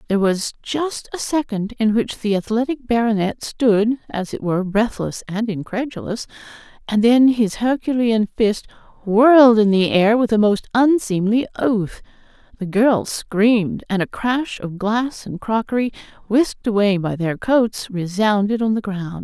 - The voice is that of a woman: Yes, female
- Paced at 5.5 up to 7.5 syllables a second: No, 4.4 syllables/s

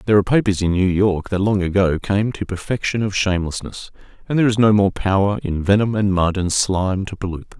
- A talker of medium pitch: No, low, 100 Hz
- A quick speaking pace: Yes, fast, 230 wpm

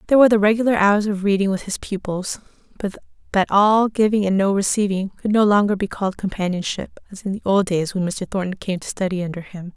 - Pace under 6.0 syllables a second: No, 6.1 syllables/s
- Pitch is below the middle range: No, high, 200 Hz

